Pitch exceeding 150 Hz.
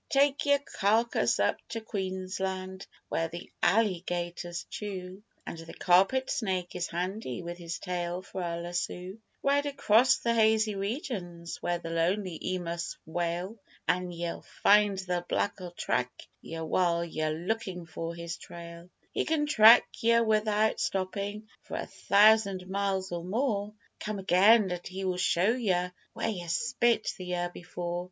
Yes: medium, 185 Hz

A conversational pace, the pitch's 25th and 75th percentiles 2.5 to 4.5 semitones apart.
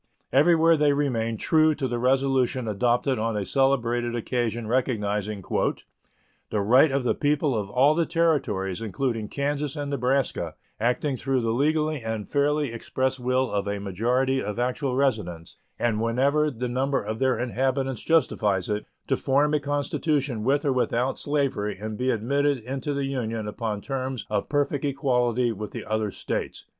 Yes: average, 160 wpm; average, 3.9 semitones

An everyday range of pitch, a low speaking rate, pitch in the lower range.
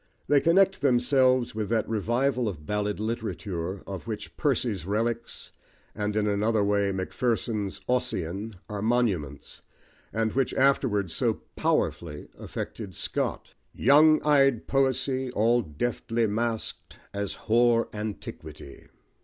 Yes: average, 3.6 semitones; slow, 115 wpm; low, 110 Hz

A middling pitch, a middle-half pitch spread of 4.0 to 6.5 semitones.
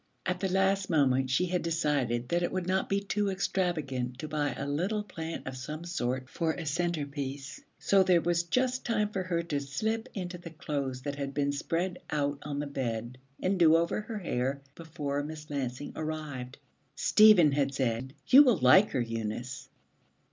Yes: medium, 155 Hz; average, 5.0 semitones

